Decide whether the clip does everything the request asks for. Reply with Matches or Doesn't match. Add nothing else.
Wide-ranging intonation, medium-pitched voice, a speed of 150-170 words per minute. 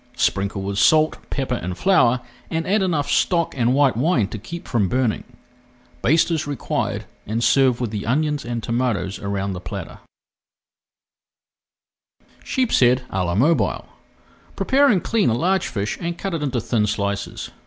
Doesn't match